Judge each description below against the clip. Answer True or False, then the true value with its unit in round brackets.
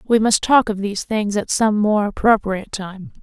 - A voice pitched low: False (210 Hz)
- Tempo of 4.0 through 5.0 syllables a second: True (4.9 syllables/s)